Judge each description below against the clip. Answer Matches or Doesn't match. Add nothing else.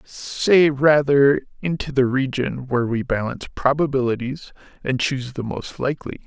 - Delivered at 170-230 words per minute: Doesn't match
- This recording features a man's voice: Matches